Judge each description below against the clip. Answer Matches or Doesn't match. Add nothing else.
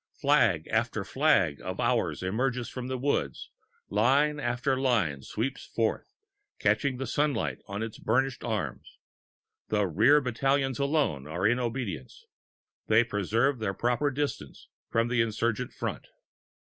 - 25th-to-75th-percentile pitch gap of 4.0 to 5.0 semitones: Matches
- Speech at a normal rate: Doesn't match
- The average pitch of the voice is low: Matches